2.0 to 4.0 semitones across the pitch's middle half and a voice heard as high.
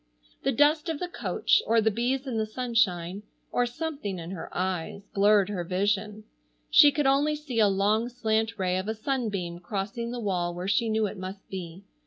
No: average, 4.4 semitones; high, 215 Hz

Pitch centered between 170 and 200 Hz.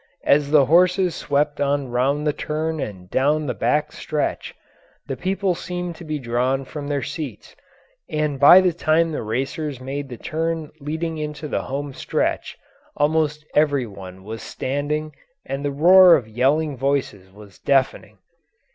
No: medium, 145 Hz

